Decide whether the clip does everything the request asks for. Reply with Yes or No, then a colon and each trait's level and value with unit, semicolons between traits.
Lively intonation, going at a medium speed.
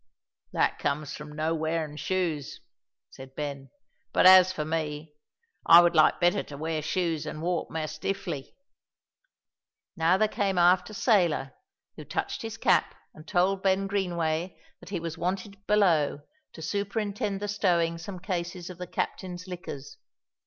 No: average, 3.3 semitones; average, 150 wpm